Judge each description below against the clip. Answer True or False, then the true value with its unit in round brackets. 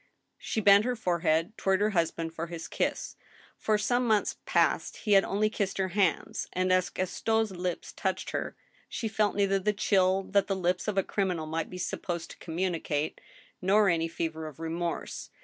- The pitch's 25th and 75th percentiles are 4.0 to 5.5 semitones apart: False (3.4 semitones)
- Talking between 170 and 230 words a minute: True (185 wpm)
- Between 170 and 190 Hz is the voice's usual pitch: True (185 Hz)